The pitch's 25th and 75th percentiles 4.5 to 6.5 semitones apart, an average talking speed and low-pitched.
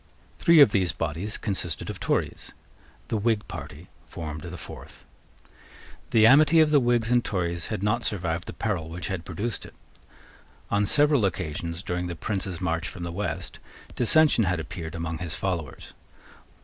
Yes: average, 4.9 semitones; average, 160 wpm; very low, 95 Hz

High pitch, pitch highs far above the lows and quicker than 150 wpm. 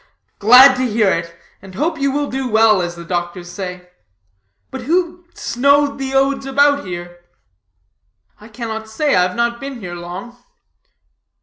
Yes: high, 235 Hz; wide, 7.2 semitones; average, 160 wpm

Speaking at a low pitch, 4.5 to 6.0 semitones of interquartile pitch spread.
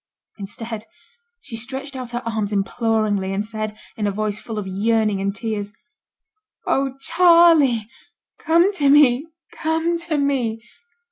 No: high, 230 Hz; average, 5.1 semitones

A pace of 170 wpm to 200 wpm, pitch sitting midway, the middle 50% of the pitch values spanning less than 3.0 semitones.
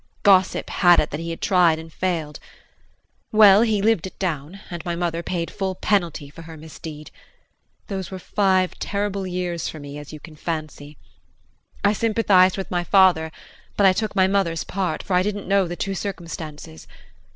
No: average, 180 wpm; medium, 180 Hz; average, 3.3 semitones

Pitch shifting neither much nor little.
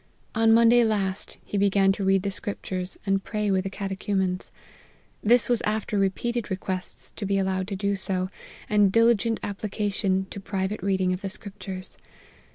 No: narrow, 1.8 semitones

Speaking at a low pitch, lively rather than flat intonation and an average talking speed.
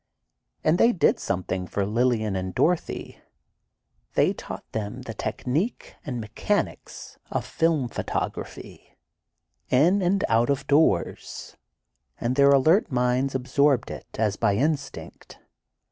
No: low, 130 Hz; wide, 6.0 semitones; slow, 120 wpm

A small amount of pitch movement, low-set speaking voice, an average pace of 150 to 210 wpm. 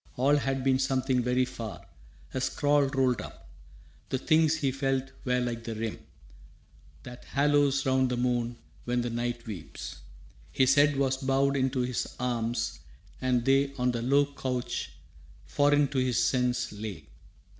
Yes: narrow, 2.0 semitones; low, 130 Hz; average, 155 wpm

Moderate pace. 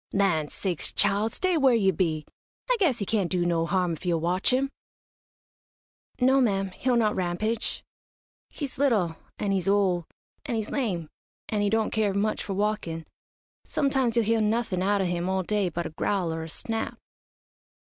Yes: average, 180 wpm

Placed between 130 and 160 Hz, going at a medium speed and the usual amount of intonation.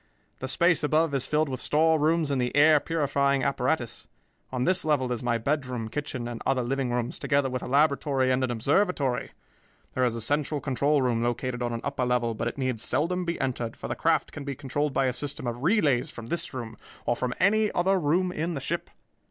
No: low, 135 Hz; fast, 215 wpm; average, 3.8 semitones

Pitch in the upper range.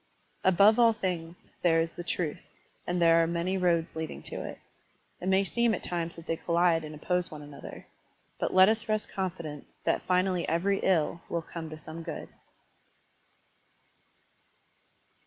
No: medium, 175 Hz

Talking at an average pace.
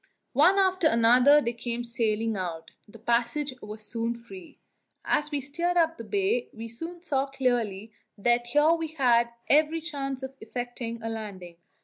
Yes: average, 160 wpm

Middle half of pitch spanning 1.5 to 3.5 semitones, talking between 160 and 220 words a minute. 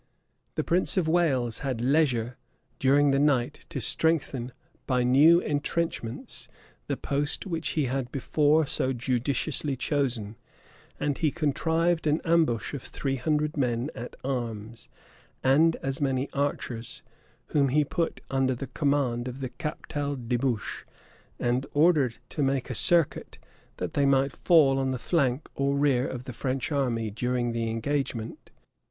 No: average, 3.2 semitones; average, 145 wpm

